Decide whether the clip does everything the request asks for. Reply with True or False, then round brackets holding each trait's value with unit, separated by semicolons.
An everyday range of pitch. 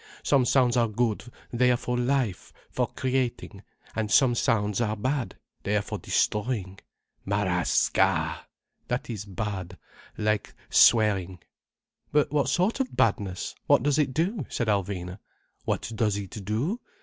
True (4.1 semitones)